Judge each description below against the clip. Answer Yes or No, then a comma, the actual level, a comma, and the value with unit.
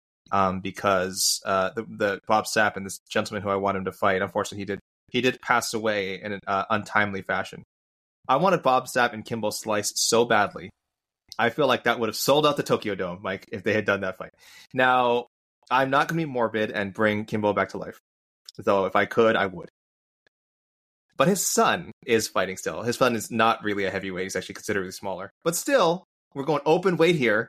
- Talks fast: Yes, fast, 215 wpm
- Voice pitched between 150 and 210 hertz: No, low, 105 Hz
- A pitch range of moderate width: Yes, average, 4.0 semitones